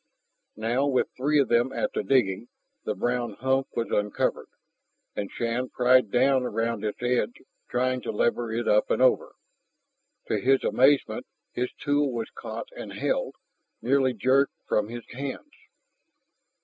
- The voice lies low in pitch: Yes, low, 125 Hz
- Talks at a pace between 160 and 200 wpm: No, average, 150 wpm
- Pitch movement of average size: No, narrow, 2.3 semitones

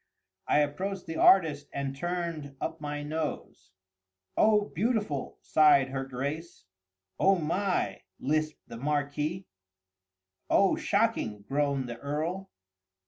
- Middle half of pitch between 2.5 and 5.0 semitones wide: Yes, average, 4.2 semitones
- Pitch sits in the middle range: Yes, medium, 150 Hz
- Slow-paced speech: Yes, slow, 110 wpm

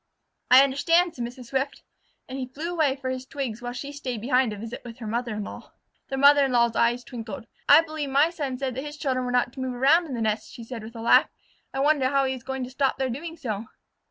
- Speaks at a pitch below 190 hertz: No, very high, 260 Hz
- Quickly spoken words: Yes, fast, 255 wpm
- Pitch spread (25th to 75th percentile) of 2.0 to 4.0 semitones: Yes, average, 2.8 semitones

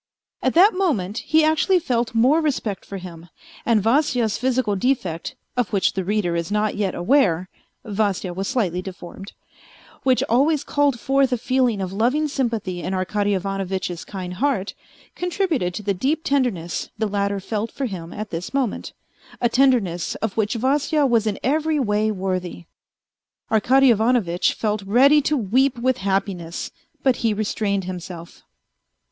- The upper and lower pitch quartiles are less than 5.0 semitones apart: No, wide, 5.6 semitones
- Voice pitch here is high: Yes, high, 215 Hz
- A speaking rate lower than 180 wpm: Yes, average, 155 wpm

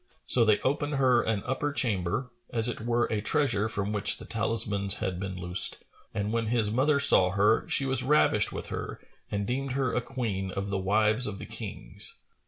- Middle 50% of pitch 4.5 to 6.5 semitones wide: No, average, 4.0 semitones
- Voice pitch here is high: No, low, 110 Hz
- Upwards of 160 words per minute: Yes, average, 195 wpm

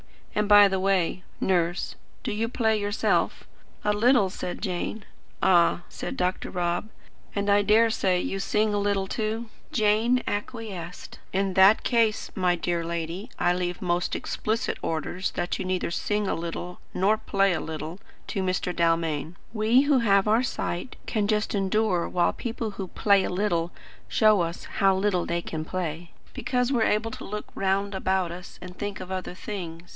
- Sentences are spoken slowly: No, average, 175 wpm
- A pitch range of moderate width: Yes, average, 3.1 semitones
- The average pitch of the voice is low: No, high, 195 Hz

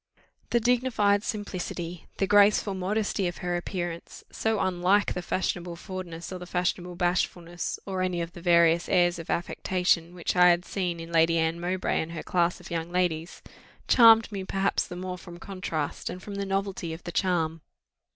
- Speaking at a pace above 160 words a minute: Yes, average, 180 wpm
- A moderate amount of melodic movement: No, narrow, 2.1 semitones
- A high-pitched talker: No, medium, 180 Hz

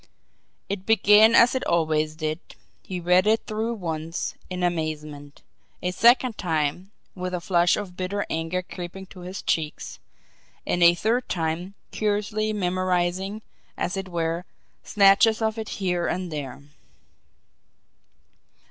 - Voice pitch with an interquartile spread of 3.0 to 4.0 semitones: Yes, average, 3.5 semitones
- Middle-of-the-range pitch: Yes, medium, 180 Hz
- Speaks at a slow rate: Yes, slow, 130 wpm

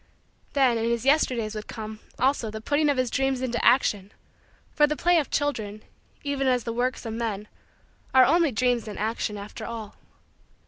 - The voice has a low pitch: No, high, 245 Hz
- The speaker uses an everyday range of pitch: Yes, average, 3.9 semitones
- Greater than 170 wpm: Yes, average, 180 wpm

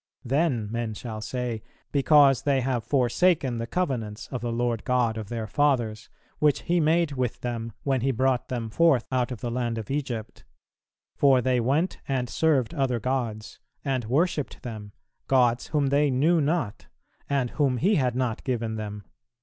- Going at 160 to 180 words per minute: Yes, average, 170 wpm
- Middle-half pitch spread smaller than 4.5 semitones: Yes, average, 3.3 semitones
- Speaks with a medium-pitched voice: No, low, 125 Hz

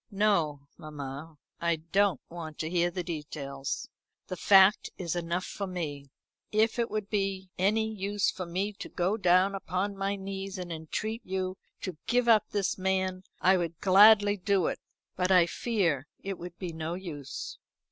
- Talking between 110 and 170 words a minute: Yes, average, 165 wpm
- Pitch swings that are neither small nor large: Yes, average, 3.0 semitones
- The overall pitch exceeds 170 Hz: Yes, medium, 185 Hz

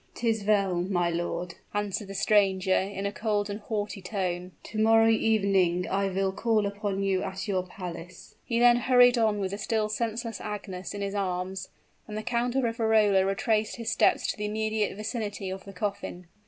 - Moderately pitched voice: No, high, 205 Hz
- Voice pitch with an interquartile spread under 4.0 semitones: Yes, narrow, 2.4 semitones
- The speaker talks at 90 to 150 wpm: No, average, 185 wpm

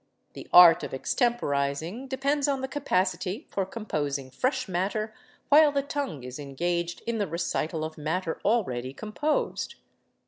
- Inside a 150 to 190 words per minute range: No, average, 140 wpm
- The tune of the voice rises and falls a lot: Yes, wide, 8.5 semitones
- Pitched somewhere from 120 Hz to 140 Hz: No, medium, 185 Hz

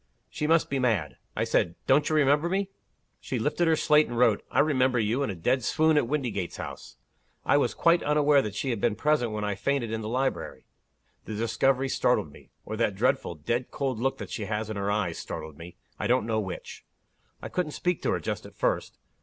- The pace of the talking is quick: Yes, fast, 220 wpm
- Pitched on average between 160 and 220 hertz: No, low, 125 Hz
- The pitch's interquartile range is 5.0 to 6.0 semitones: Yes, wide, 5.6 semitones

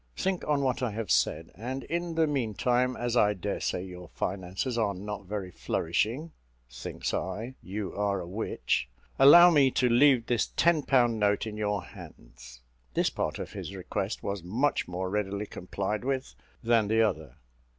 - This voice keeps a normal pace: Yes, average, 170 wpm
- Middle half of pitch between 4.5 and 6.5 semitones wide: Yes, average, 5.2 semitones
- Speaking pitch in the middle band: No, low, 105 Hz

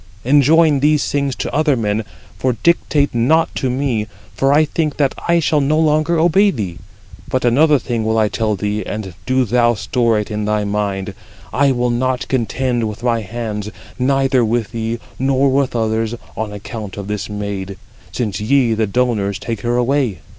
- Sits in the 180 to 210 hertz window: No, low, 120 Hz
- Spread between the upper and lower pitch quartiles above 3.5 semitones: Yes, average, 4.4 semitones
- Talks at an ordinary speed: Yes, average, 180 wpm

